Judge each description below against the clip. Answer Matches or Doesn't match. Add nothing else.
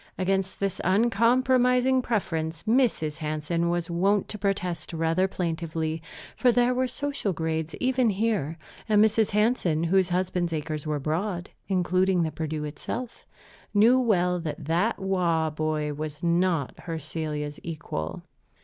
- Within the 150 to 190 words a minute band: Doesn't match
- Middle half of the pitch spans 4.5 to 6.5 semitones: Matches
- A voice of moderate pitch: Matches